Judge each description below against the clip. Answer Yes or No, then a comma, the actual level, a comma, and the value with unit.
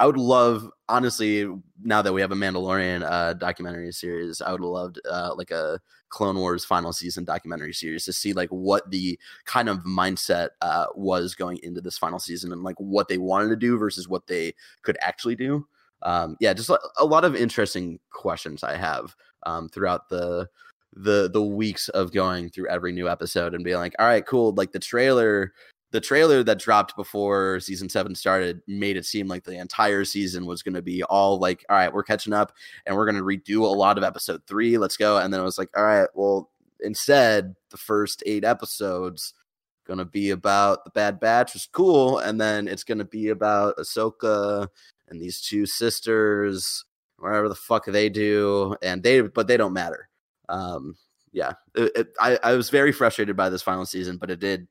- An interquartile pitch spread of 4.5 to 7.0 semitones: No, narrow, 2.6 semitones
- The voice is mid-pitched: No, very low, 95 Hz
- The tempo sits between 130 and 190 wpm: No, average, 200 wpm